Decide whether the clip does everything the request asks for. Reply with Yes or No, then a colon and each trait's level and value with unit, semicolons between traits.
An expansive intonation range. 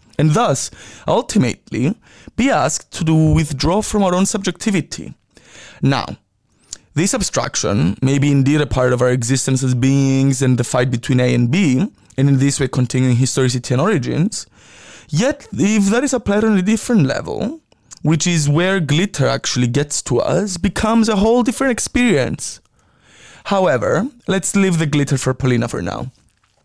Yes: wide, 7.3 semitones